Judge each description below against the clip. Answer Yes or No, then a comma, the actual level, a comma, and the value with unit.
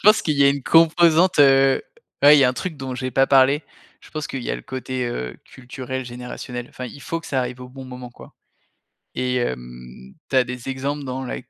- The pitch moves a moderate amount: No, narrow, 2.1 semitones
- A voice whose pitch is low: Yes, low, 130 Hz